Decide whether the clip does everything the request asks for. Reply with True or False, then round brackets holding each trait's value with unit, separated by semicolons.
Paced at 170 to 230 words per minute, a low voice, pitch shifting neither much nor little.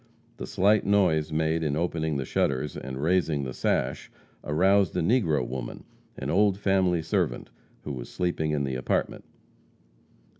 False (150 wpm; 80 Hz; 4.8 semitones)